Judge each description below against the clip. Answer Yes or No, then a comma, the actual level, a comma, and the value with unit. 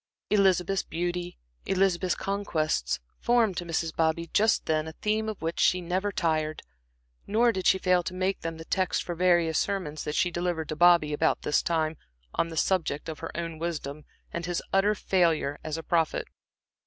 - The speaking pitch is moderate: Yes, medium, 175 Hz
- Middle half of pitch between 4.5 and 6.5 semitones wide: No, average, 2.8 semitones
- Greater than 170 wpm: Yes, average, 180 wpm